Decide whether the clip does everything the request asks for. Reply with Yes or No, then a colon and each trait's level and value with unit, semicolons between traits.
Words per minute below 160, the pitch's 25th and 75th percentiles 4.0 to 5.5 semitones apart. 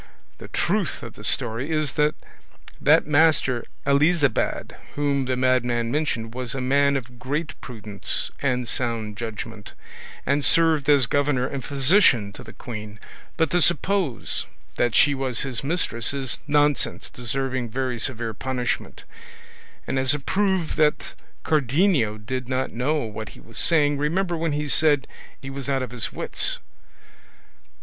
No: average, 150 wpm; average, 3.5 semitones